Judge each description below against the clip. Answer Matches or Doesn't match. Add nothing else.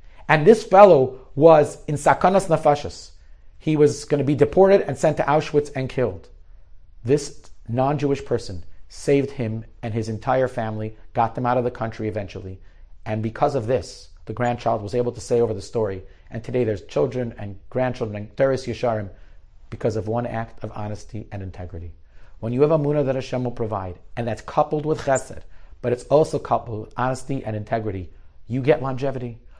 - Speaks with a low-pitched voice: Matches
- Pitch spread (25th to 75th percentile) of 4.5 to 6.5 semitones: Matches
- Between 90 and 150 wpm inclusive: Doesn't match